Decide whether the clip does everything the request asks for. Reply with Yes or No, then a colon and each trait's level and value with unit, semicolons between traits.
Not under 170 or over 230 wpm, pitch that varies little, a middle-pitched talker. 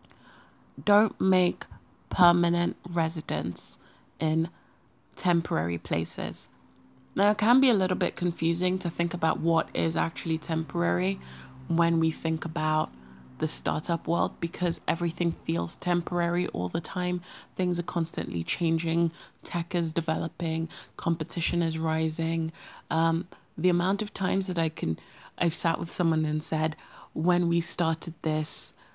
No: slow, 135 wpm; narrow, 1.7 semitones; medium, 165 Hz